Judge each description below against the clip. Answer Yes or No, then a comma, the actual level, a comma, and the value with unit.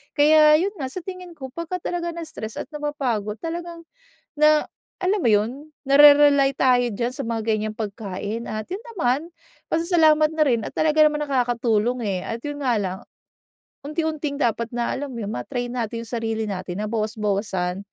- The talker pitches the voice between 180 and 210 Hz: No, very high, 255 Hz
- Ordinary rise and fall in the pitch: No, wide, 5.7 semitones